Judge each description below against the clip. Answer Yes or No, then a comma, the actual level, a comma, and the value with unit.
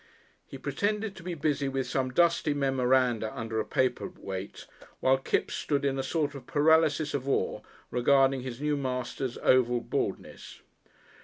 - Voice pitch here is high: No, low, 135 Hz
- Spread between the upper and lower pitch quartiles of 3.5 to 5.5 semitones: No, average, 2.8 semitones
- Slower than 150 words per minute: No, average, 155 wpm